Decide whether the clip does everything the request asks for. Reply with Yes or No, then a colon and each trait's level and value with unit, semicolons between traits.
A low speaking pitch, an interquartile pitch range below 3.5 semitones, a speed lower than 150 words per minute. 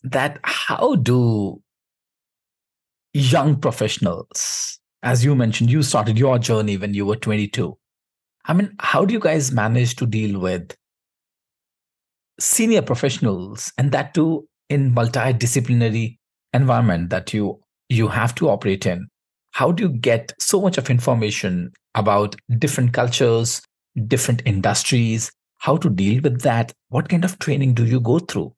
No: low, 120 Hz; average, 4.0 semitones; average, 140 wpm